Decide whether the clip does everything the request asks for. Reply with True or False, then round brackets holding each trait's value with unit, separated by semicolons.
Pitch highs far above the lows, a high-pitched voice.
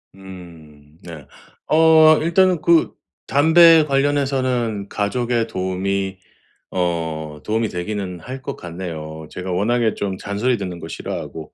False (7.1 semitones; 100 Hz)